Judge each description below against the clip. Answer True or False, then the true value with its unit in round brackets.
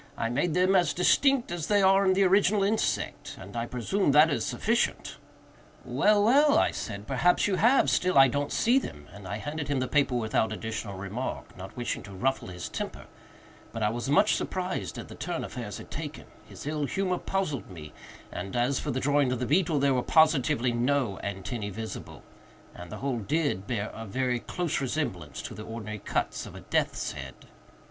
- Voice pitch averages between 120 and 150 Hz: True (135 Hz)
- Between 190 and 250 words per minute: True (195 wpm)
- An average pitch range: False (8.3 semitones)